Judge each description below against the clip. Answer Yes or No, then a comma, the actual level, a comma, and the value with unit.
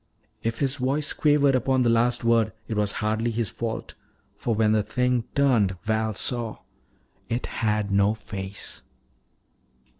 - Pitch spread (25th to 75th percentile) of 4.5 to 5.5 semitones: No, average, 2.8 semitones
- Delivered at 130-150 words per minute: Yes, average, 145 wpm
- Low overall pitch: Yes, low, 115 Hz